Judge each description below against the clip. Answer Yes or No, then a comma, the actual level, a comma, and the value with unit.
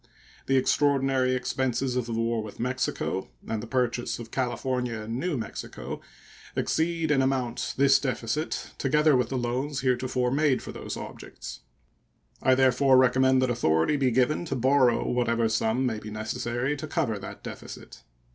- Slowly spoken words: No, average, 160 wpm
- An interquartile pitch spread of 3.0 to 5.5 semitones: No, narrow, 2.4 semitones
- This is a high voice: No, low, 130 Hz